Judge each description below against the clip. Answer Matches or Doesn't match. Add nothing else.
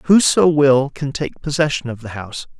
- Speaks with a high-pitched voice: Doesn't match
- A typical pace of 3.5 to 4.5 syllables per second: Doesn't match